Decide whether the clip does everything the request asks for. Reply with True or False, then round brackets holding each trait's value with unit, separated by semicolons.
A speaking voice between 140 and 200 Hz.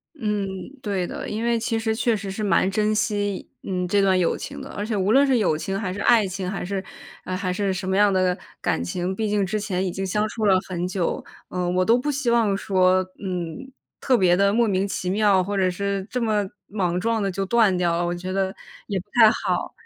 True (195 Hz)